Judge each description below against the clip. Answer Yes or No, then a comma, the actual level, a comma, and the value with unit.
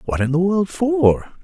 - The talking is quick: Yes, fast, 210 wpm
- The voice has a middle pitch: Yes, medium, 160 Hz